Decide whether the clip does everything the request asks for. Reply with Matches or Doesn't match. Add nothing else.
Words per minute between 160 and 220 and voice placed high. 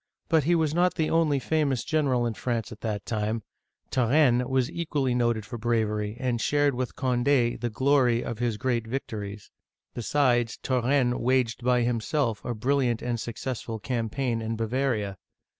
Doesn't match